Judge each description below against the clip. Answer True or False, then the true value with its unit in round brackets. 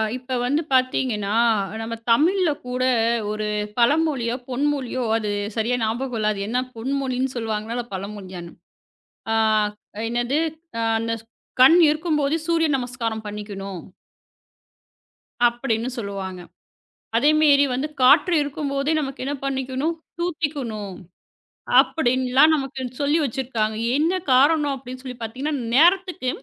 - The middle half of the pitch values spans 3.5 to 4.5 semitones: True (4.2 semitones)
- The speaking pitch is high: True (255 Hz)